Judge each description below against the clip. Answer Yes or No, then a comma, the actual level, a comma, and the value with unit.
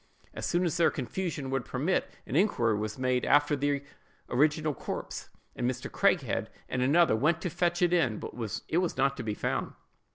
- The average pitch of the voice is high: No, medium, 145 Hz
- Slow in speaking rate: No, average, 190 wpm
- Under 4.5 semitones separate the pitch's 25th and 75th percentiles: No, average, 5.2 semitones